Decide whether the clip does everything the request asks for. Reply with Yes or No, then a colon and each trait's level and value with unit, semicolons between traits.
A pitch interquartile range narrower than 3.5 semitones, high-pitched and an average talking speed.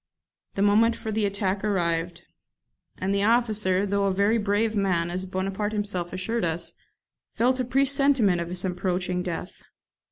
Yes: average, 3.1 semitones; high, 200 Hz; average, 155 wpm